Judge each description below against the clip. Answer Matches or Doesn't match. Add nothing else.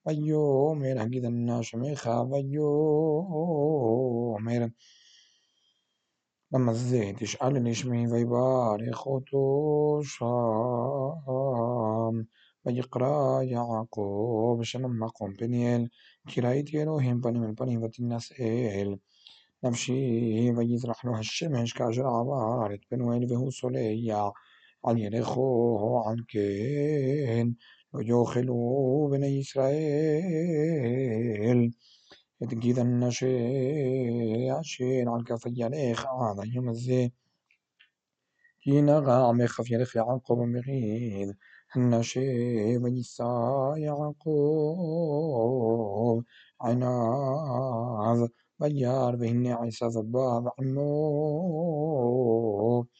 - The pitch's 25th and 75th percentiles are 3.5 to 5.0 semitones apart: Doesn't match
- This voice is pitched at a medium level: Doesn't match